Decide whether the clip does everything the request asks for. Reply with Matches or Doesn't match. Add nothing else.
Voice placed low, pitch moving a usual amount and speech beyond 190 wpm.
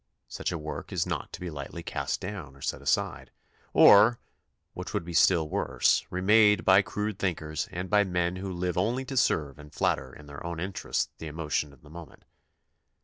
Matches